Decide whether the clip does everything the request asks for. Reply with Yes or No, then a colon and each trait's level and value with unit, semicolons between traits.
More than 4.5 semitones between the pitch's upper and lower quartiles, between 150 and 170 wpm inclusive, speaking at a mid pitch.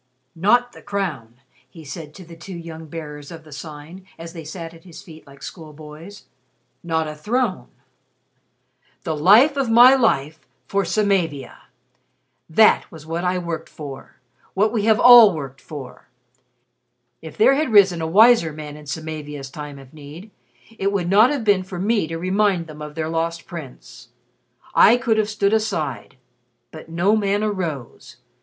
Yes: average, 5.0 semitones; average, 165 wpm; medium, 170 Hz